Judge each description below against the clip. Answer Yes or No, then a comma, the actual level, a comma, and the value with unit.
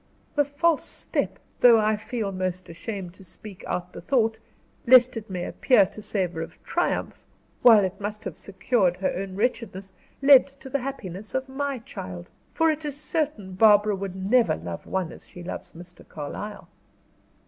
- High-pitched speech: Yes, high, 210 Hz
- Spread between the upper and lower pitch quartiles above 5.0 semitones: Yes, wide, 5.4 semitones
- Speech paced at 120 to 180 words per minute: Yes, average, 170 wpm